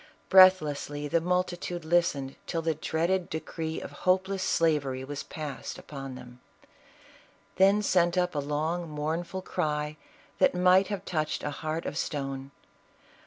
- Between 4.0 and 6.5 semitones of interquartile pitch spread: No, average, 3.5 semitones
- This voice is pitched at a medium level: Yes, medium, 160 Hz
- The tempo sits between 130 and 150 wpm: Yes, slow, 135 wpm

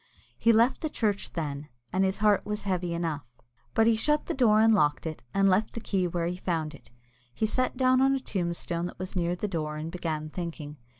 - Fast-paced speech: Yes, fast, 225 wpm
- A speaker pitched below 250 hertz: Yes, medium, 185 Hz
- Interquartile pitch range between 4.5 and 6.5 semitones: Yes, average, 4.8 semitones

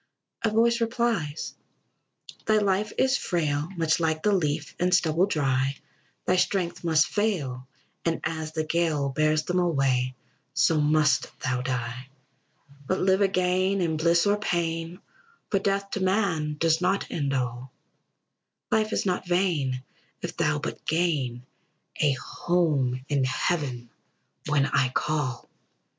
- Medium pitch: Yes, medium, 160 Hz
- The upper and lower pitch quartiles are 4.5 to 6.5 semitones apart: Yes, average, 4.8 semitones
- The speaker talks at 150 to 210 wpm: No, average, 140 wpm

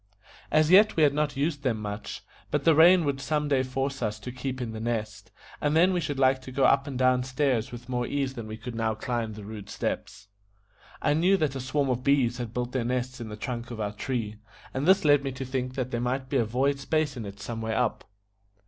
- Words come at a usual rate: No, fast, 250 wpm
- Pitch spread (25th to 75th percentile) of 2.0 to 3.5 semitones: Yes, average, 3.2 semitones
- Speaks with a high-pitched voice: No, low, 130 Hz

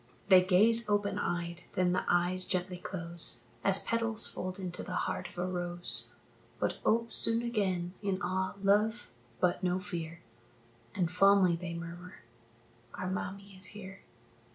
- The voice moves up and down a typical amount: No, narrow, 2.3 semitones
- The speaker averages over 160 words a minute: No, average, 150 wpm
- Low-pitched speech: No, medium, 185 Hz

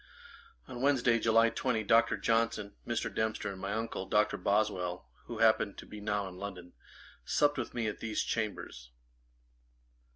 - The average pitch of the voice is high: No, low, 110 Hz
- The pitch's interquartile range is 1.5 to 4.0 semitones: Yes, narrow, 2.4 semitones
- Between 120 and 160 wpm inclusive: Yes, average, 155 wpm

